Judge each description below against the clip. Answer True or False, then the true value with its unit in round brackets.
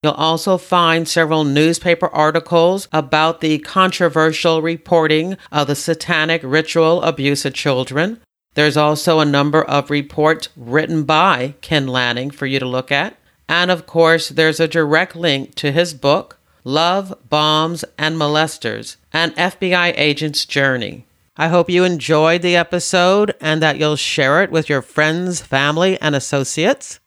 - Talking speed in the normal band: True (150 wpm)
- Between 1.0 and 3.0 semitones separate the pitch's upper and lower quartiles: True (2.4 semitones)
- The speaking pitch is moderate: True (160 Hz)